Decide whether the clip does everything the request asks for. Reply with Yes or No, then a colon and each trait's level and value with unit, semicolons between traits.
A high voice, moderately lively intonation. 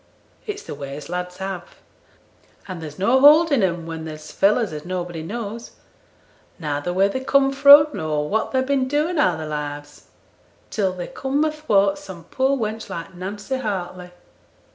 No: high, 195 Hz; wide, 7.9 semitones